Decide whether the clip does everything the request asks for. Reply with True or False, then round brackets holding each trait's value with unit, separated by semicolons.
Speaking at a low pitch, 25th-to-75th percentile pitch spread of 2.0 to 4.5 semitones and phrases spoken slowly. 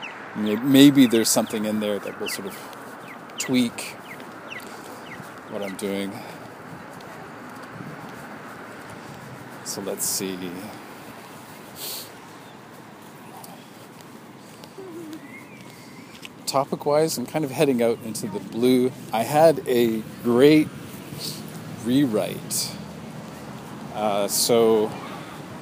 False (125 Hz; 5.6 semitones; 75 wpm)